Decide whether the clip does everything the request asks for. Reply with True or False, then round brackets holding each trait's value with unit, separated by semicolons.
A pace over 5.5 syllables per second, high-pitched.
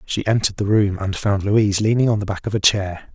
False (6.0 syllables/s; 105 Hz)